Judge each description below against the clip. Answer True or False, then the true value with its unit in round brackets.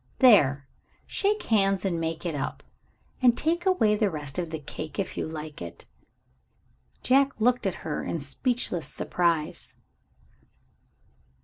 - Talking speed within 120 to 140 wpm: True (135 wpm)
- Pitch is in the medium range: True (180 Hz)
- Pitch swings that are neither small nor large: False (7.7 semitones)